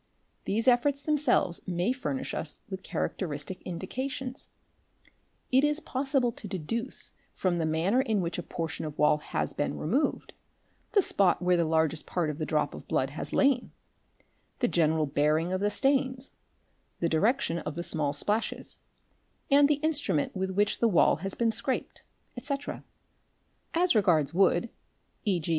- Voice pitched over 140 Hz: Yes, high, 190 Hz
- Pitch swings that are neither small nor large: No, wide, 8.2 semitones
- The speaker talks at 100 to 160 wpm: Yes, average, 155 wpm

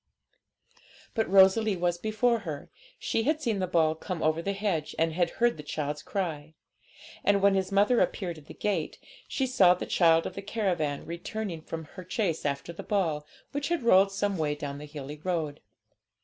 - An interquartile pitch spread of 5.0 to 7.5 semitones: No, average, 4.5 semitones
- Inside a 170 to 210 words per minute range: Yes, average, 190 wpm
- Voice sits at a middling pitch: Yes, medium, 180 Hz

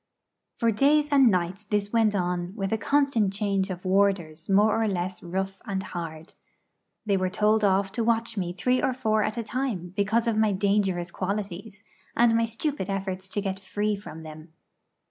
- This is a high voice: Yes, high, 200 Hz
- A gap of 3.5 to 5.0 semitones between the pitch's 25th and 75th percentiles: No, average, 3.1 semitones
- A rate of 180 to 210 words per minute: Yes, average, 185 wpm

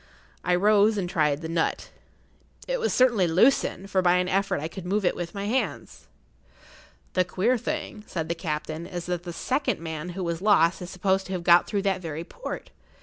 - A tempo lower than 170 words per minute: No, fast, 205 wpm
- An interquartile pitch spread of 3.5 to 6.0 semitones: No, average, 3.1 semitones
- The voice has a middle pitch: Yes, medium, 180 Hz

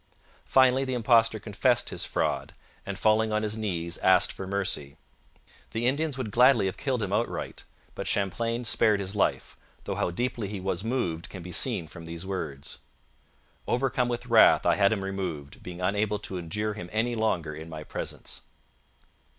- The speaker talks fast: No, average, 175 wpm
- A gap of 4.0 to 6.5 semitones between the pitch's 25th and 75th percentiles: Yes, average, 4.3 semitones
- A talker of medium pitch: No, low, 105 Hz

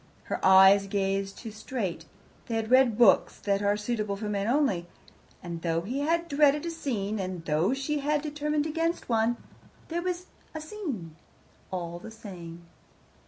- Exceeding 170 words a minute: No, average, 165 wpm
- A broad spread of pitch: Yes, wide, 7.3 semitones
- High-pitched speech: Yes, high, 220 Hz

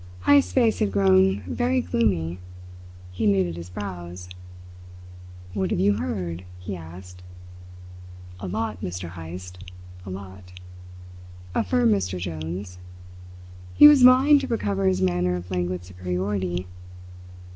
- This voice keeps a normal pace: No, slow, 120 wpm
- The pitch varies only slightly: Yes, narrow, 2.1 semitones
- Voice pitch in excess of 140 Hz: No, very low, 95 Hz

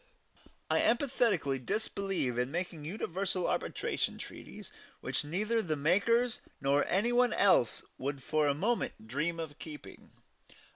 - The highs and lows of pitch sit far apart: Yes, wide, 6.6 semitones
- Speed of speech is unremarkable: No, slow, 130 wpm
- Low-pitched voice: No, medium, 170 Hz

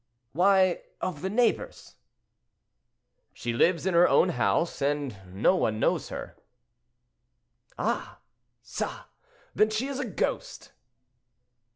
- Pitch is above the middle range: No, medium, 180 Hz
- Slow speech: Yes, slow, 110 wpm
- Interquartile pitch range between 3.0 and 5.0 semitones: No, wide, 5.4 semitones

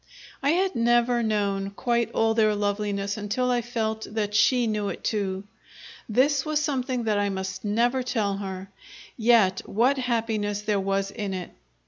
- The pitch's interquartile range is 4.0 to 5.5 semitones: No, average, 3.1 semitones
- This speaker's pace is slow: No, average, 160 wpm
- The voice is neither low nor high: No, high, 220 Hz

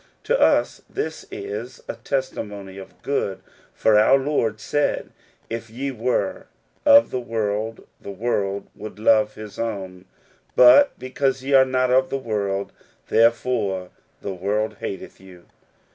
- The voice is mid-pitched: No, low, 115 Hz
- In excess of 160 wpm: No, average, 145 wpm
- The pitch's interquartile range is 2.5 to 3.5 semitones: No, average, 4.7 semitones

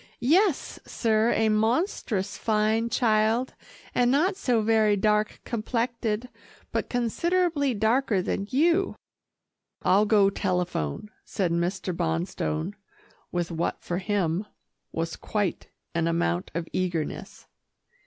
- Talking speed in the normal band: No, slow, 110 wpm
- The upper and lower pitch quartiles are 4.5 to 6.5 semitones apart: Yes, average, 4.9 semitones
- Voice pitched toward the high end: Yes, high, 215 Hz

